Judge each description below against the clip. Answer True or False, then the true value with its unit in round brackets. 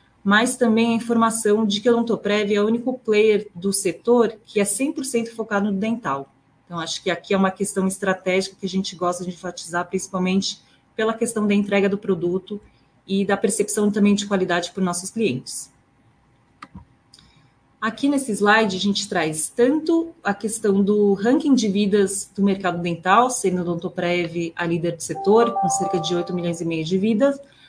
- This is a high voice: True (200 Hz)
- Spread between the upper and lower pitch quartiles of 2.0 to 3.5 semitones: True (3.1 semitones)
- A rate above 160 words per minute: True (175 wpm)